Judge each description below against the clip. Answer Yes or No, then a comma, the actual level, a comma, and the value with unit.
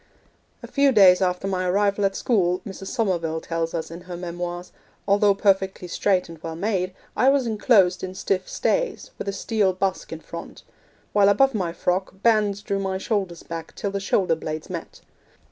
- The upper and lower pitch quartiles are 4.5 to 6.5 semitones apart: No, narrow, 2.4 semitones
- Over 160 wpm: Yes, average, 180 wpm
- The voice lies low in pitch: No, high, 190 Hz